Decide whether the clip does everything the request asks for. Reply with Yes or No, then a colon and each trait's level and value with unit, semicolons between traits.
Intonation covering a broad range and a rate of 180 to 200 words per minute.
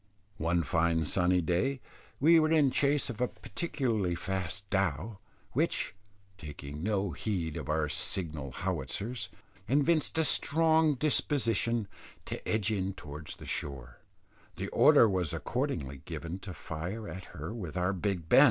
No: wide, 7.0 semitones; average, 145 wpm